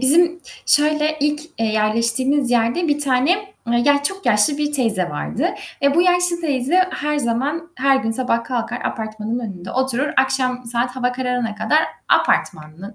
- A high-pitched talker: Yes, very high, 260 Hz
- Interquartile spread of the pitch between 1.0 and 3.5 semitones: No, average, 4.3 semitones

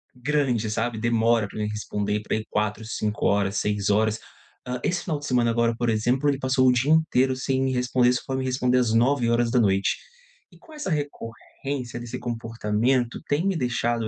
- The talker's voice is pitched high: No, low, 120 Hz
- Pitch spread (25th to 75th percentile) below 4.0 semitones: Yes, average, 3.0 semitones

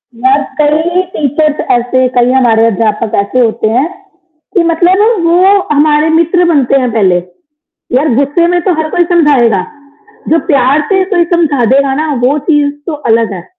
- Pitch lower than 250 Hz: No, very high, 285 Hz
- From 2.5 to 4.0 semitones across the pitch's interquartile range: No, average, 4.9 semitones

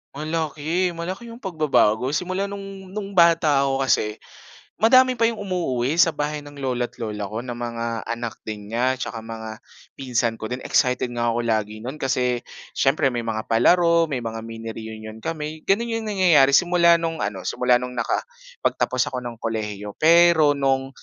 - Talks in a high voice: No, low, 135 Hz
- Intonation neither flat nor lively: No, wide, 6.6 semitones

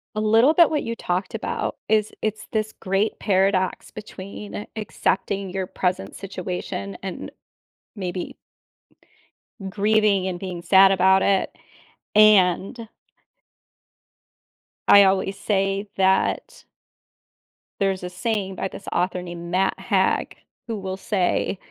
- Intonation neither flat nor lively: No, narrow, 2.2 semitones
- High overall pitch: Yes, high, 195 Hz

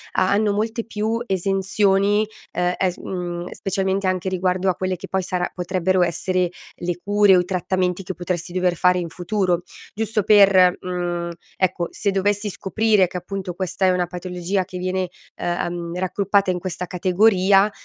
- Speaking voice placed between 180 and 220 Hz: Yes, medium, 185 Hz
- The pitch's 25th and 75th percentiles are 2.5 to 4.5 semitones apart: No, narrow, 1.7 semitones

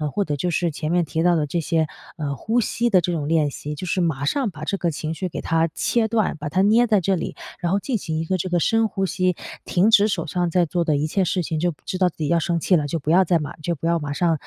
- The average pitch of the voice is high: No, medium, 170 Hz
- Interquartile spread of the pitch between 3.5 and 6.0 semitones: No, average, 3.1 semitones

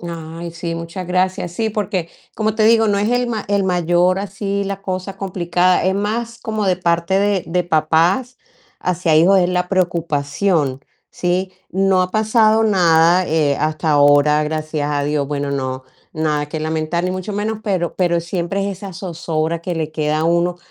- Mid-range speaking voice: Yes, medium, 175 Hz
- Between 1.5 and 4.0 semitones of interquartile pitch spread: Yes, average, 3.6 semitones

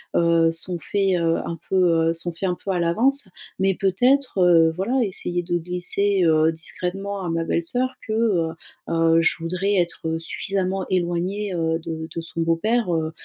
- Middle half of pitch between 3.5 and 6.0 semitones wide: No, average, 2.8 semitones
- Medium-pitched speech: Yes, medium, 175 Hz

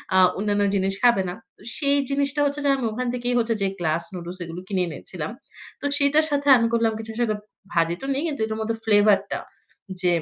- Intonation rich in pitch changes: Yes, wide, 6.1 semitones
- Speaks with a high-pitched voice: Yes, high, 220 Hz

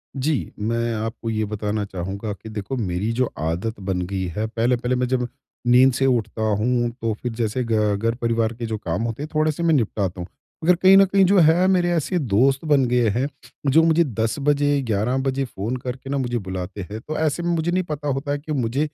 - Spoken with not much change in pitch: No, average, 4.8 semitones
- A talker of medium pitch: No, low, 120 Hz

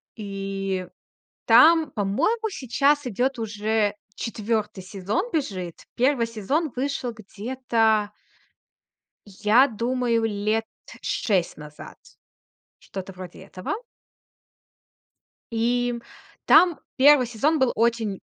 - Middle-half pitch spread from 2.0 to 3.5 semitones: No, average, 4.3 semitones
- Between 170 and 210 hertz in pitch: No, high, 225 Hz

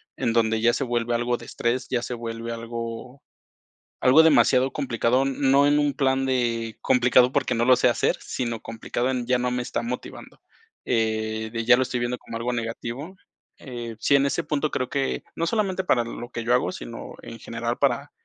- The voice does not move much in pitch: Yes, narrow, 2.3 semitones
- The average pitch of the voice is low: Yes, low, 125 Hz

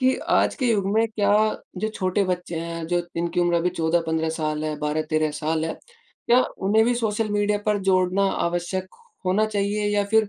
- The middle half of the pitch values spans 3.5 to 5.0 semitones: Yes, average, 4.2 semitones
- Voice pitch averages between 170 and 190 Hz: Yes, medium, 185 Hz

